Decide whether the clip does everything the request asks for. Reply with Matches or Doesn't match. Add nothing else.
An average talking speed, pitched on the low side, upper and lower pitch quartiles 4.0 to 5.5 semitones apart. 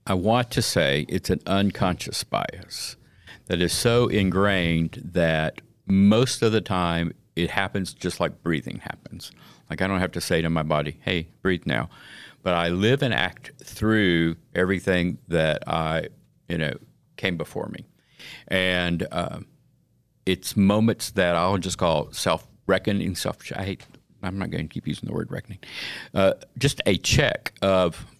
Doesn't match